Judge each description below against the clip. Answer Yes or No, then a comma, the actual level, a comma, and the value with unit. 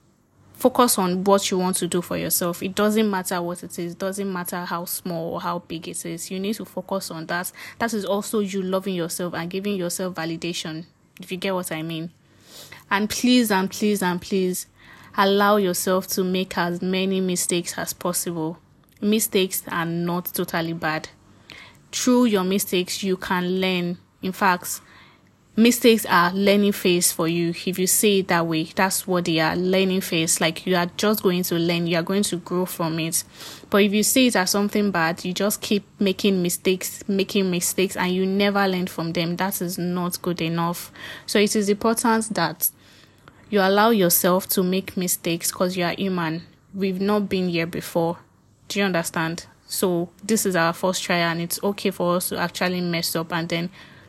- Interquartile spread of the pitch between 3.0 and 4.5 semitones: No, narrow, 2.4 semitones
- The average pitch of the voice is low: No, medium, 185 Hz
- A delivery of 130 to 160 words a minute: No, average, 190 wpm